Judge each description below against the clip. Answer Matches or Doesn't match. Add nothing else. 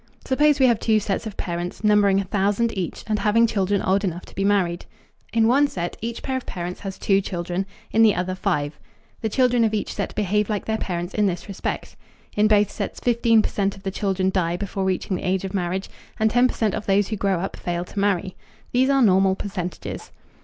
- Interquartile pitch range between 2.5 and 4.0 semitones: Matches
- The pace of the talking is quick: Matches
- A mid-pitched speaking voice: Doesn't match